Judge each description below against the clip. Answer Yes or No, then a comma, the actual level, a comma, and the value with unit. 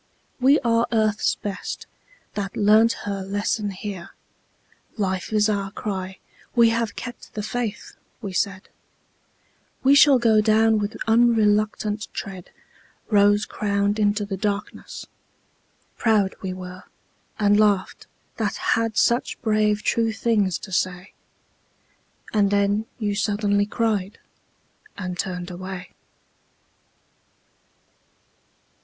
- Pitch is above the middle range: Yes, high, 210 Hz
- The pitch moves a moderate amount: No, narrow, 2.0 semitones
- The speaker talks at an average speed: No, slow, 110 wpm